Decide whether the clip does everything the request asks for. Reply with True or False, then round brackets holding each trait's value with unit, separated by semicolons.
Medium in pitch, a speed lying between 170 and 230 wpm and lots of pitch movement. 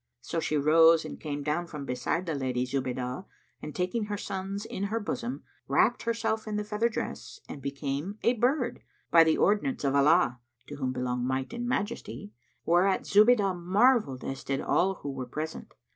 True (170 Hz; 180 wpm; 7.2 semitones)